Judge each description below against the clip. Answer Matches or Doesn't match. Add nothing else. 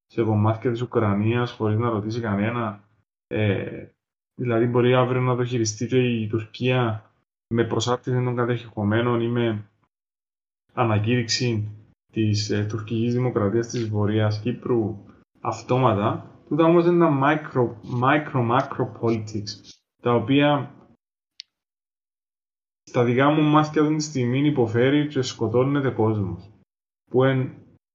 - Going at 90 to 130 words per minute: Matches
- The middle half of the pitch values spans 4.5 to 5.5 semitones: Doesn't match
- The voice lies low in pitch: Matches